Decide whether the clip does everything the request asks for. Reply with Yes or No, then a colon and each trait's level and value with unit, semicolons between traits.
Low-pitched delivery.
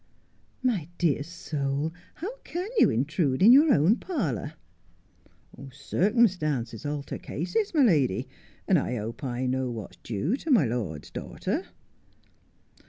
No: medium, 150 Hz